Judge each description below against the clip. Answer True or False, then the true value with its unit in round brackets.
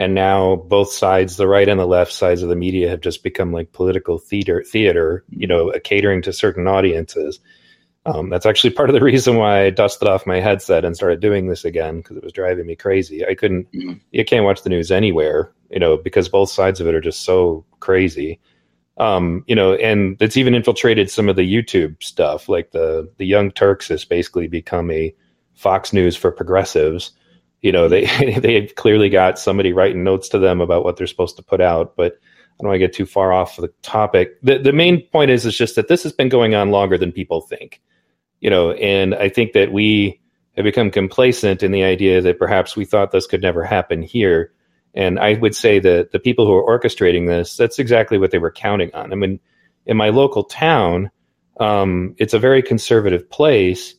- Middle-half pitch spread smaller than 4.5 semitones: False (4.9 semitones)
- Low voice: True (95 Hz)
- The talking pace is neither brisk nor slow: False (210 wpm)